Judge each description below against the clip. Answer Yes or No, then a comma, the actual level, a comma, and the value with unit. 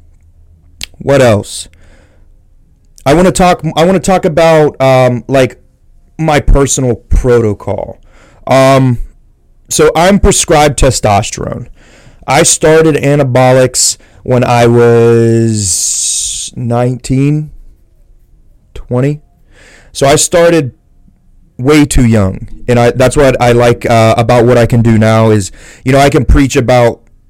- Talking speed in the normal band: No, slow, 120 wpm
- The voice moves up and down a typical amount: Yes, average, 4.5 semitones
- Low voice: Yes, low, 125 Hz